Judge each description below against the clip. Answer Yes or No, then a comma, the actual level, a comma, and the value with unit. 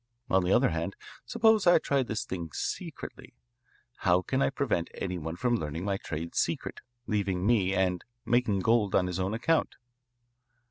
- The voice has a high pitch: No, very low, 95 Hz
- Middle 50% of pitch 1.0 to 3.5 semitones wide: No, average, 5.1 semitones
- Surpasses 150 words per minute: Yes, average, 170 wpm